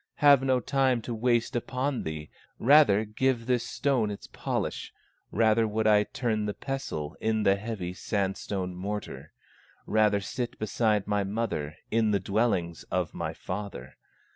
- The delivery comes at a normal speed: Yes, average, 145 wpm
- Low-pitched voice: Yes, low, 110 Hz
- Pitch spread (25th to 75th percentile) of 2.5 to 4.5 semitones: Yes, average, 3.5 semitones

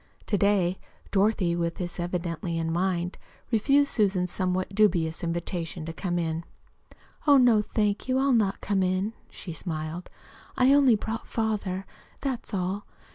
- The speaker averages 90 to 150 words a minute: Yes, average, 145 wpm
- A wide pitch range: No, average, 3.8 semitones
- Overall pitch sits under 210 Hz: Yes, high, 190 Hz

